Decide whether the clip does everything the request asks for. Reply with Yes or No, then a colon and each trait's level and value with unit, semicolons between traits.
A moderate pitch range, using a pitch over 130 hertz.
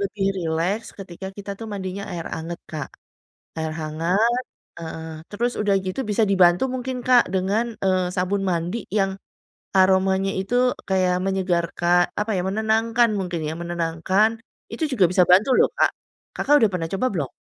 Yes: average, 3.2 semitones; high, 190 Hz